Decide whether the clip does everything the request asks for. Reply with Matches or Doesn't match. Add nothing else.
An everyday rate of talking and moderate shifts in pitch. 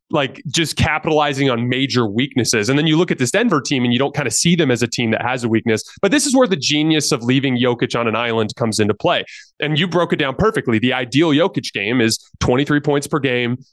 Doesn't match